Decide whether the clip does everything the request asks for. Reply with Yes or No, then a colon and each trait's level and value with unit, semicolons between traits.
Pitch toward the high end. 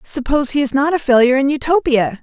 Yes: very high, 275 Hz